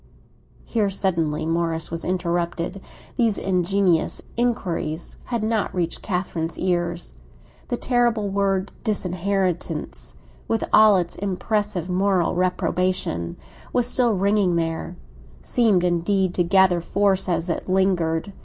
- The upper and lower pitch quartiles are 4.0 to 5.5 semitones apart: No, average, 2.8 semitones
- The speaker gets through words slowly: Yes, slow, 115 wpm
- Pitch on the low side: No, medium, 185 Hz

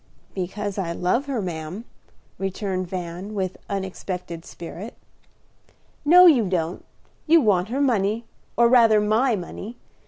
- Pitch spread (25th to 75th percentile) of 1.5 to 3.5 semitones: No, average, 4.4 semitones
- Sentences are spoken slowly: Yes, slow, 125 wpm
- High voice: Yes, high, 200 Hz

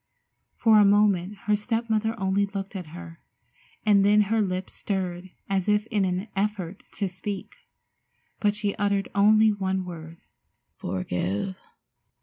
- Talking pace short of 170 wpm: Yes, average, 140 wpm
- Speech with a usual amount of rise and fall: No, narrow, 2.3 semitones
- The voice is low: No, high, 200 Hz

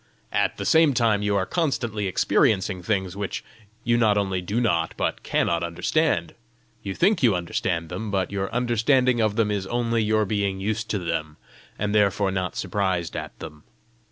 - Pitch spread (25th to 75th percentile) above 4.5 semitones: No, average, 3.5 semitones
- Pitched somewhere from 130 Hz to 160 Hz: No, low, 100 Hz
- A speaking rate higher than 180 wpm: No, average, 175 wpm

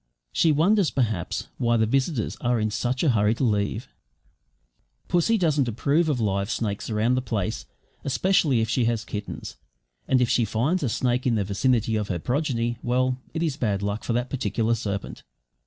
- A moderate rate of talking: Yes, average, 180 wpm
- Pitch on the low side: Yes, low, 120 Hz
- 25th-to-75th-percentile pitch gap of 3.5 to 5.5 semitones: Yes, average, 3.8 semitones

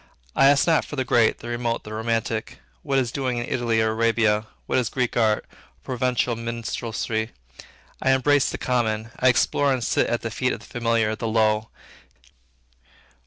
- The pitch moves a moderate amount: No, narrow, 2.3 semitones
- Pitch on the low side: Yes, low, 115 Hz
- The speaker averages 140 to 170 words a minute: No, average, 180 wpm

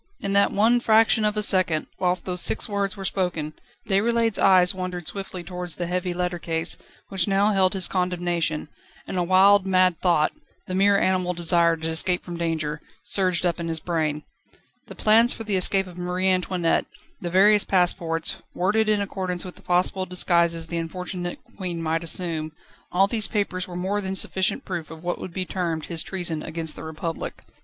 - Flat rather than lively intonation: Yes, narrow, 2.2 semitones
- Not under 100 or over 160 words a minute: No, average, 185 wpm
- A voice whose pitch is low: No, medium, 180 Hz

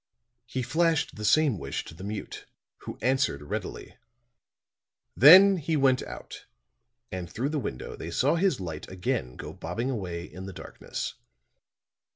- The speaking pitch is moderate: No, low, 120 Hz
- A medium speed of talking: Yes, average, 150 wpm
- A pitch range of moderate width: No, wide, 8.5 semitones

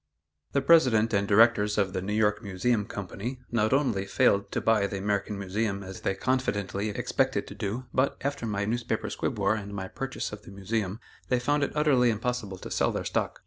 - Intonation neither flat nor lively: Yes, average, 3.6 semitones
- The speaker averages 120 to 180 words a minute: No, average, 200 wpm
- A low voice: Yes, low, 105 Hz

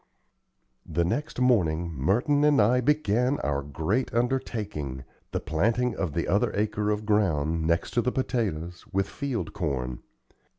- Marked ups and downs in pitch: Yes, wide, 7.4 semitones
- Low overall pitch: Yes, low, 105 Hz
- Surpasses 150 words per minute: No, average, 140 wpm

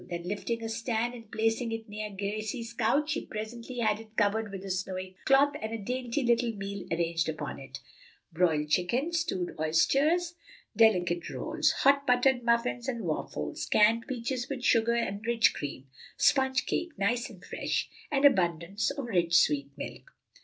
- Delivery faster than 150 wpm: Yes, average, 165 wpm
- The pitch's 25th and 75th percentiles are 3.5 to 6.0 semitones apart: Yes, average, 4.9 semitones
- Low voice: No, high, 225 Hz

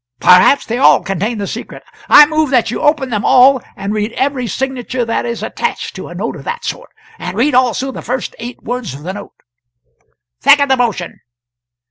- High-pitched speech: Yes, high, 245 Hz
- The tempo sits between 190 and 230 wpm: Yes, average, 195 wpm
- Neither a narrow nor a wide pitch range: Yes, average, 4.2 semitones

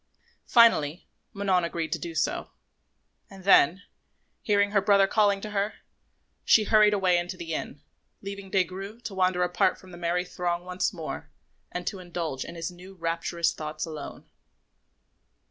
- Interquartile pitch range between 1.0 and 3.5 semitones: Yes, average, 2.7 semitones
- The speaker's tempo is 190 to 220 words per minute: No, average, 160 wpm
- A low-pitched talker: No, medium, 180 Hz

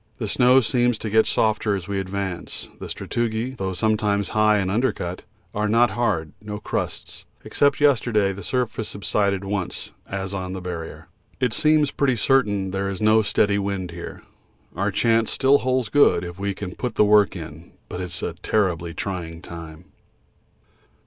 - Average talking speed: Yes, average, 170 wpm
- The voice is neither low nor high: No, low, 100 Hz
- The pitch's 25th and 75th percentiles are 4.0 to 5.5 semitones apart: No, average, 3.4 semitones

